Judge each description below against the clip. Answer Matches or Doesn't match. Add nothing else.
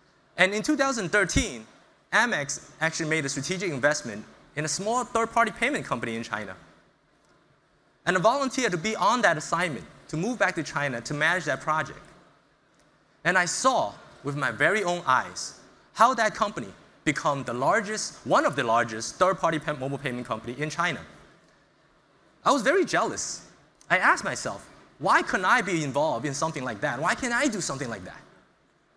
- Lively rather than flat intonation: Matches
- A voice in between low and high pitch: Matches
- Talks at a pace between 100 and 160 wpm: Doesn't match